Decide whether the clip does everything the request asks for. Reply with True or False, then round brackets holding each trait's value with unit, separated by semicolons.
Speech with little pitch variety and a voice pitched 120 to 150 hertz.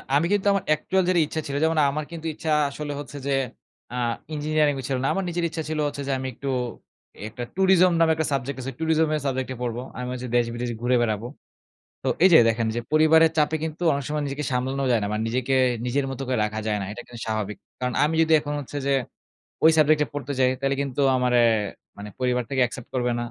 False (4.0 semitones; 140 Hz)